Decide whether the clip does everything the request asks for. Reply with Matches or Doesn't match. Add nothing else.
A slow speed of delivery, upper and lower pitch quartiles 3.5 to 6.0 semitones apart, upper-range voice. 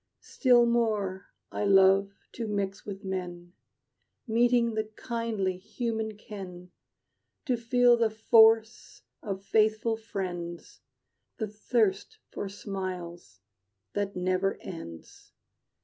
Doesn't match